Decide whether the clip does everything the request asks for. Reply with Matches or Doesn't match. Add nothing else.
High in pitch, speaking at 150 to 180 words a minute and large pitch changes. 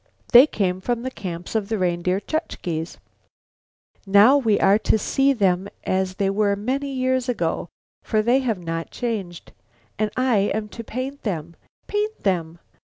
Matches